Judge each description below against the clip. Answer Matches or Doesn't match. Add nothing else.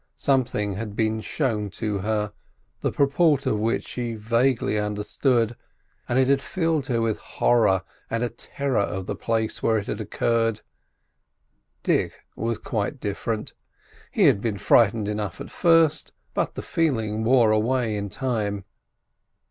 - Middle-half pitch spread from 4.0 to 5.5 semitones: Doesn't match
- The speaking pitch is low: Matches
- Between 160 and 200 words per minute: Doesn't match